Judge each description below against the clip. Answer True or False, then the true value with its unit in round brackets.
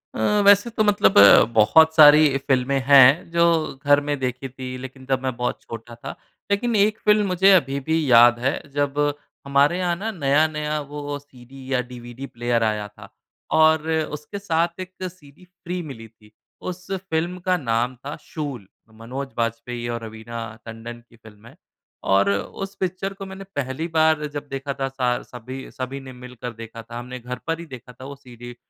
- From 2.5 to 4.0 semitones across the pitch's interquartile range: False (4.9 semitones)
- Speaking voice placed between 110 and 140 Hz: True (135 Hz)